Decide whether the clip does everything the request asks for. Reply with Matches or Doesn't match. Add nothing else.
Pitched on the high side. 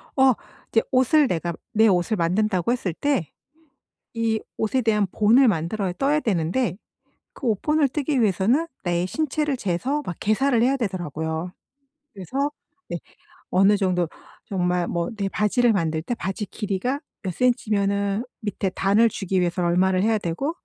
Matches